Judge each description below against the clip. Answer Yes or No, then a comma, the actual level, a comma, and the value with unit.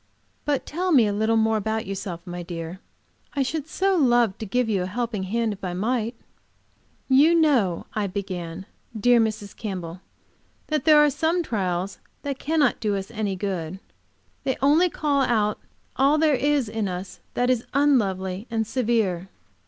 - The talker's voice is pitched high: Yes, high, 220 Hz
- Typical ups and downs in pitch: No, wide, 6.2 semitones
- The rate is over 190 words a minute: No, average, 170 wpm